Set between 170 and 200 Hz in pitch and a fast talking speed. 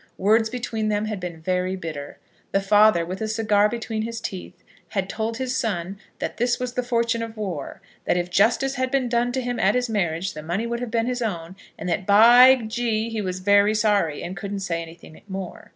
No: high, 215 Hz; fast, 215 wpm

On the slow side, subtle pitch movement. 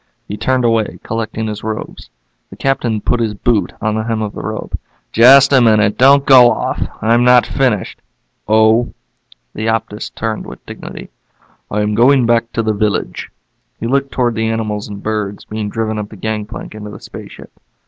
No: average, 180 wpm; narrow, 2.0 semitones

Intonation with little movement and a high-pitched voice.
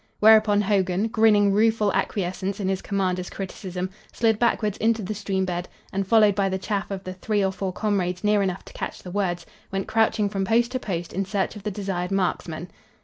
Yes: narrow, 2.2 semitones; high, 195 Hz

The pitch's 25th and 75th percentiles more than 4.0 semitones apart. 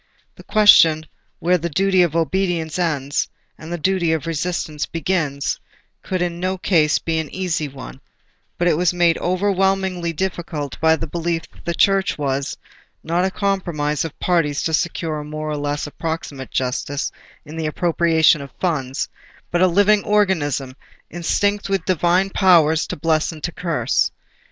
No: average, 3.1 semitones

